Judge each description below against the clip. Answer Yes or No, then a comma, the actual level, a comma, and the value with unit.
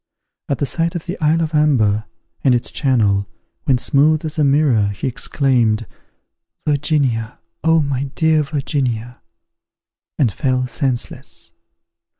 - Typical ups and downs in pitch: Yes, average, 4.1 semitones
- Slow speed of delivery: Yes, slow, 130 wpm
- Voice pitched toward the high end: No, low, 135 Hz